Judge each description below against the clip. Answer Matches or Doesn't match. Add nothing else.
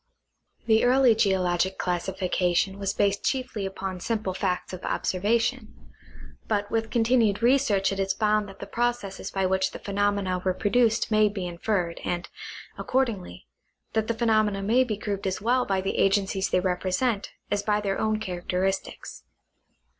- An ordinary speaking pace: Matches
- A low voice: Doesn't match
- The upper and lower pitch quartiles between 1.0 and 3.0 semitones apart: Matches